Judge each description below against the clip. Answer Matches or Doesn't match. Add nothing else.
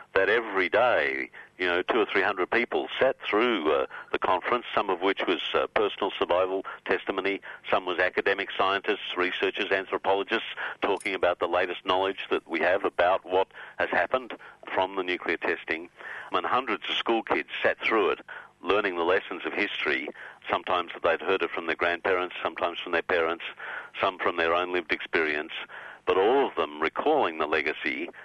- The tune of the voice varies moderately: Doesn't match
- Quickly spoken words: Doesn't match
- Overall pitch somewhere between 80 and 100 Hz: Matches